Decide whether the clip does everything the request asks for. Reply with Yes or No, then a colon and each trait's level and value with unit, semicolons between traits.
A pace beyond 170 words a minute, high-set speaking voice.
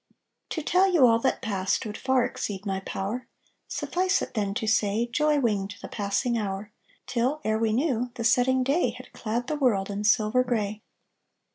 Yes: average, 180 wpm; high, 230 Hz